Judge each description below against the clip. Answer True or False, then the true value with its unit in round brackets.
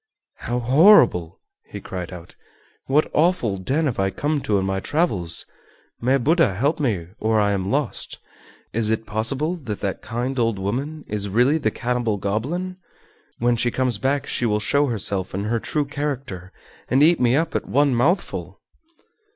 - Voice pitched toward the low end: True (120 Hz)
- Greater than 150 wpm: True (170 wpm)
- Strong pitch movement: True (6.0 semitones)